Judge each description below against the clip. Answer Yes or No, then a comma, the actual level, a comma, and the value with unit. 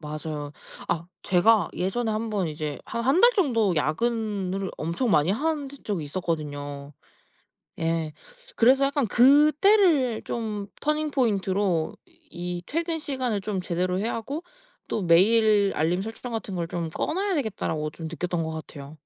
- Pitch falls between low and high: No, high, 200 Hz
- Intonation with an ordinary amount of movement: No, wide, 7.2 semitones